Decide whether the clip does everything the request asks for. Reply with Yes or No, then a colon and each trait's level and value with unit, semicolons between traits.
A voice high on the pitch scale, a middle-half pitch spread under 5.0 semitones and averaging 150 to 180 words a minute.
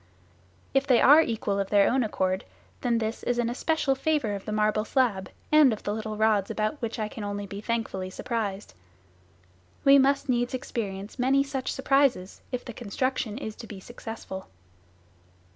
Yes: high, 225 Hz; average, 4.2 semitones; average, 170 wpm